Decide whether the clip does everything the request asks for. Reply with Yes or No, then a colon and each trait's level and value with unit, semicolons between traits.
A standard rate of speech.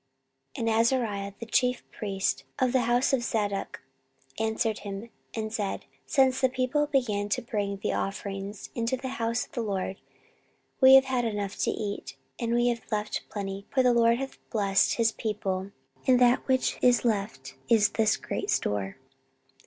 Yes: average, 170 wpm